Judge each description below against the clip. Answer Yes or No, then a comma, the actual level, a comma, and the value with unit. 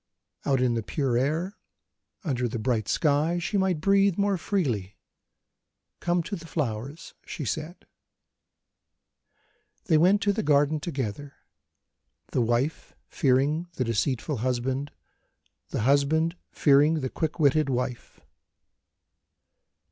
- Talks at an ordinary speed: No, slow, 115 wpm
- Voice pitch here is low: No, medium, 145 Hz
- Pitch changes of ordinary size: Yes, average, 4.6 semitones